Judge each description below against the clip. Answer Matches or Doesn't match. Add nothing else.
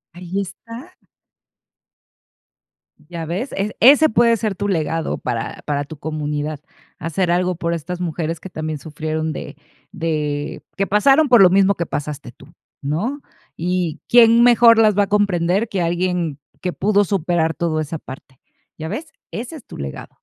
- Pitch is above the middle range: Doesn't match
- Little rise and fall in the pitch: Doesn't match